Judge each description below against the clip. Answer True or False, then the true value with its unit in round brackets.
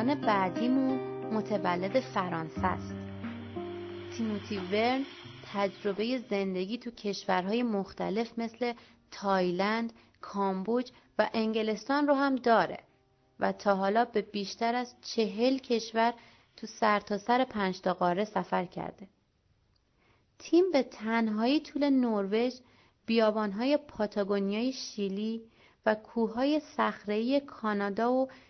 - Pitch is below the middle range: False (220 Hz)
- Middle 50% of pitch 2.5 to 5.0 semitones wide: True (3.5 semitones)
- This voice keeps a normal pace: False (100 wpm)